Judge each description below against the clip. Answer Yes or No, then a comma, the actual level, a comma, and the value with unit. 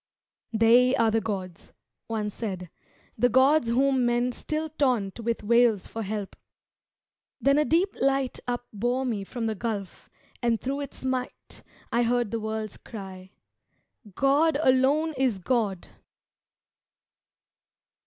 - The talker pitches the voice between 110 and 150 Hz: No, high, 240 Hz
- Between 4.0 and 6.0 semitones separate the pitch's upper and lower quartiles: No, average, 3.5 semitones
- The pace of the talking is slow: Yes, slow, 125 wpm